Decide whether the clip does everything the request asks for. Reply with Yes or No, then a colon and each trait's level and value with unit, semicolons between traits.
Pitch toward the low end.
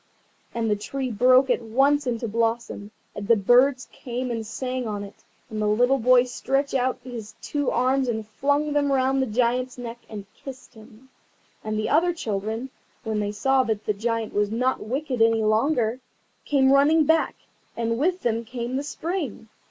No: high, 245 Hz